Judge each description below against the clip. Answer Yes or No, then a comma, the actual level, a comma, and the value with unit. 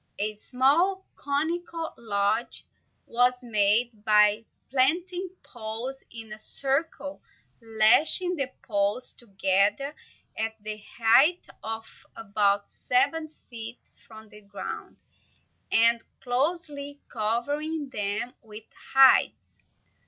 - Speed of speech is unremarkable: No, slow, 95 wpm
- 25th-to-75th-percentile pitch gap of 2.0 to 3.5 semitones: No, average, 4.9 semitones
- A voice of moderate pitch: No, high, 235 Hz